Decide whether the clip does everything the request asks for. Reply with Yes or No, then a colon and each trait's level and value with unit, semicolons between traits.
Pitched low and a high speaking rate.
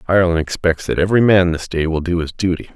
Yes: very low, 90 Hz; fast, 240 wpm